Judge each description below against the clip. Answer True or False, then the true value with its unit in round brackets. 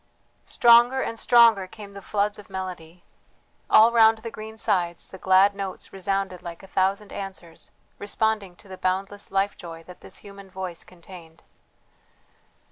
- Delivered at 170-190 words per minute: False (150 wpm)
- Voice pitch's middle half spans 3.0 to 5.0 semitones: False (2.4 semitones)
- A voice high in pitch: True (195 Hz)